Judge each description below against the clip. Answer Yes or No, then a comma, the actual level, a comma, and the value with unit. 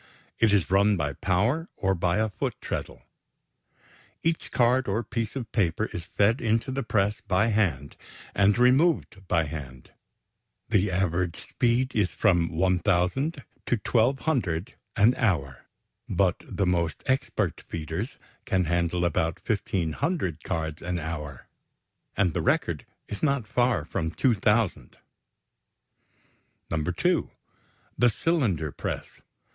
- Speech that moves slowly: Yes, slow, 125 wpm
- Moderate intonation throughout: No, wide, 5.7 semitones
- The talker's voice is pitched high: No, low, 100 Hz